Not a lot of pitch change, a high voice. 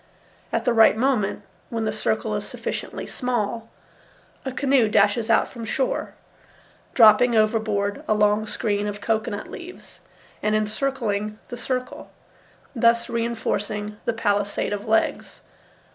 Yes: narrow, 2.2 semitones; high, 220 Hz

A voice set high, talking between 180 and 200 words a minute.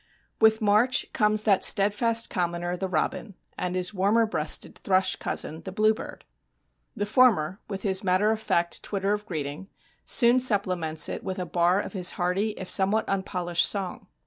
No: high, 195 Hz; average, 165 wpm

